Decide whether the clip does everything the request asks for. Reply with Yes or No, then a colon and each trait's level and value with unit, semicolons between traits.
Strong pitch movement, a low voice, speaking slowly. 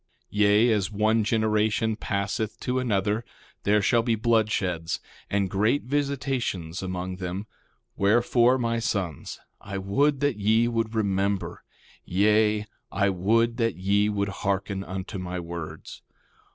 No: average, 2.9 semitones; low, 105 Hz; slow, 130 wpm